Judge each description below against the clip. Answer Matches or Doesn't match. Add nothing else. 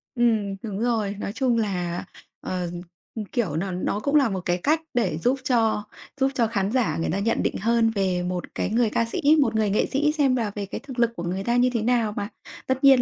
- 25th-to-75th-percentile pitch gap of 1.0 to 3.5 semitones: Doesn't match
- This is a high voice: Matches